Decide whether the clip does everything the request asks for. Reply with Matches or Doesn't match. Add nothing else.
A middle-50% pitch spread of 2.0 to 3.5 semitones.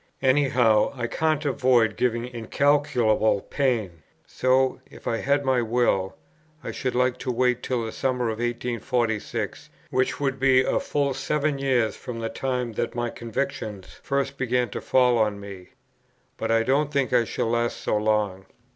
Matches